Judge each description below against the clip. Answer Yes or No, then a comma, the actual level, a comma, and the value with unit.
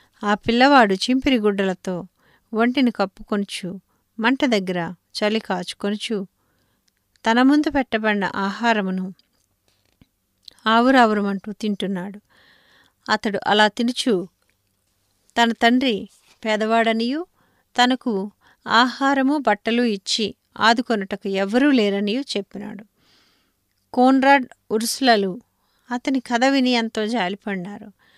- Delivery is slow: Yes, slow, 80 wpm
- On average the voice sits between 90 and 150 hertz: No, high, 215 Hz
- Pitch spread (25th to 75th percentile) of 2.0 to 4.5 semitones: Yes, average, 3.6 semitones